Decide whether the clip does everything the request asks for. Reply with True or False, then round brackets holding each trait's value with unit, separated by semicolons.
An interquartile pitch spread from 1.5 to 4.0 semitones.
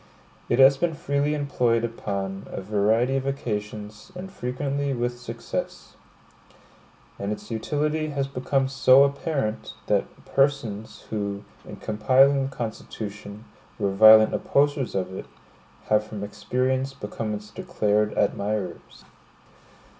False (4.6 semitones)